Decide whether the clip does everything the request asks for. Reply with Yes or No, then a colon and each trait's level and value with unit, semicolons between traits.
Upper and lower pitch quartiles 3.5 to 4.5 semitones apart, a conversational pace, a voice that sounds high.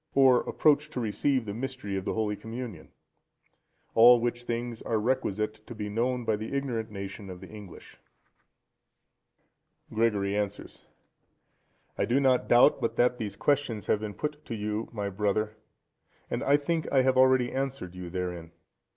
No: average, 3.9 semitones; average, 160 wpm; low, 115 Hz